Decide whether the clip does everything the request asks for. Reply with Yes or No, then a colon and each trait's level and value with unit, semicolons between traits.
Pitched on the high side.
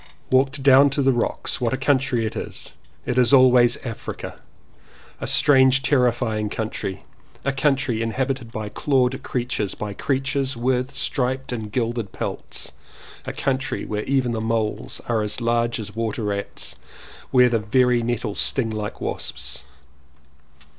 No: low, 125 Hz